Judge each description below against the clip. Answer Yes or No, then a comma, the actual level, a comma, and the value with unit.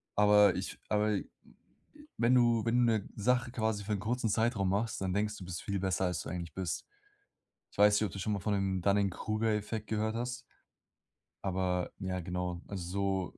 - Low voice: Yes, low, 100 Hz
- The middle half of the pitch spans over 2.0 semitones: Yes, average, 2.7 semitones